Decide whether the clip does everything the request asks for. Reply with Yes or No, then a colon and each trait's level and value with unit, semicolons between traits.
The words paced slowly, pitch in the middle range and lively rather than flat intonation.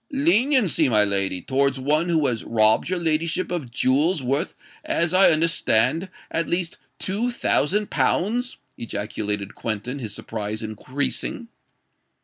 Yes: slow, 125 wpm; medium, 145 Hz; wide, 8.6 semitones